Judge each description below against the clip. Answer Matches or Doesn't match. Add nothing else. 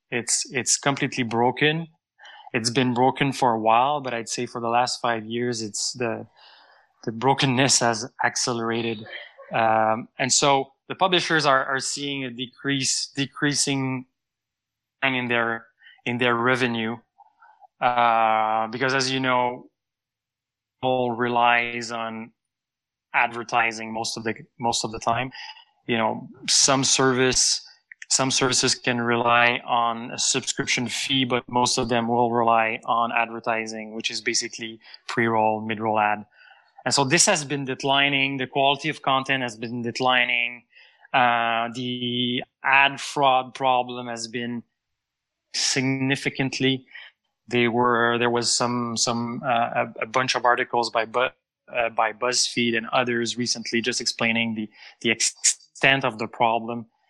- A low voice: Matches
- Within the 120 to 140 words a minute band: Matches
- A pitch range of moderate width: Doesn't match